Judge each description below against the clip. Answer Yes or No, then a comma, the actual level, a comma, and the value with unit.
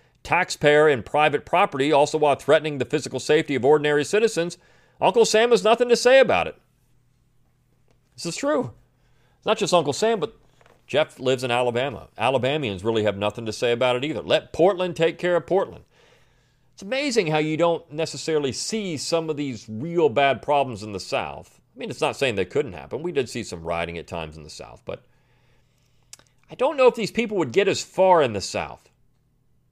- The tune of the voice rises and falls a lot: Yes, wide, 5.8 semitones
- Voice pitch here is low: No, medium, 145 Hz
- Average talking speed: Yes, average, 195 wpm